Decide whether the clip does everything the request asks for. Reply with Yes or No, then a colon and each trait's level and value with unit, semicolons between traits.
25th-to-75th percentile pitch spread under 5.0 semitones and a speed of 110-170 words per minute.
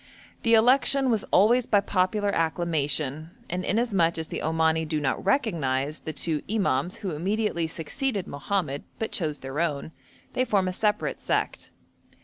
No: average, 5.3 semitones; average, 150 wpm